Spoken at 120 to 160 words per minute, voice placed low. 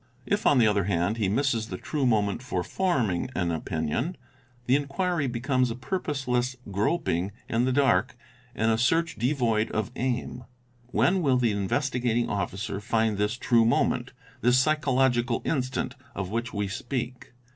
Yes: average, 155 wpm; low, 120 Hz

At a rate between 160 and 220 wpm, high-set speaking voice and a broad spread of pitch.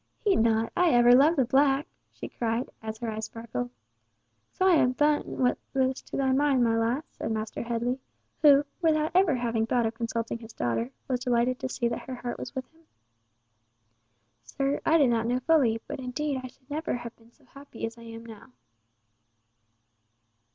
No: average, 185 wpm; very high, 250 Hz; average, 3.4 semitones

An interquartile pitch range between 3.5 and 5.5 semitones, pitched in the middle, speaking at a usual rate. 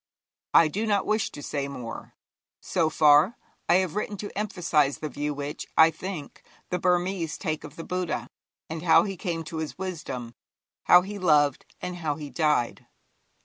Yes: average, 3.8 semitones; medium, 160 Hz; average, 175 wpm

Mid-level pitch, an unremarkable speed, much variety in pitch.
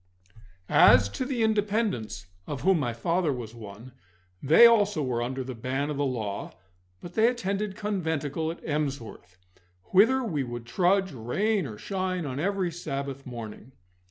Yes: medium, 150 Hz; average, 155 wpm; wide, 8.0 semitones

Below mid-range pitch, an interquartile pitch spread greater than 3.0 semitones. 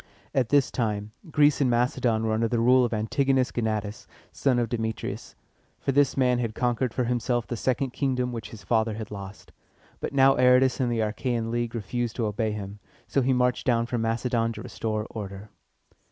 No: low, 120 Hz; narrow, 2.4 semitones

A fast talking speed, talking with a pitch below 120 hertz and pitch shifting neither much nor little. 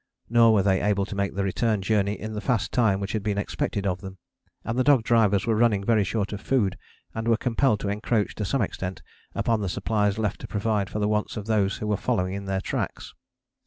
No: fast, 235 wpm; low, 105 Hz; narrow, 2.2 semitones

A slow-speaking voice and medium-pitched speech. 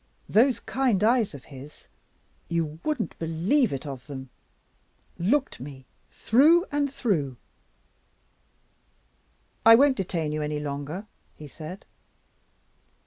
Yes: slow, 110 wpm; medium, 170 Hz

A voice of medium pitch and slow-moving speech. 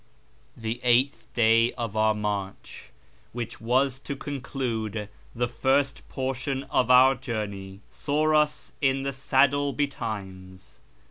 No: low, 125 Hz; slow, 120 wpm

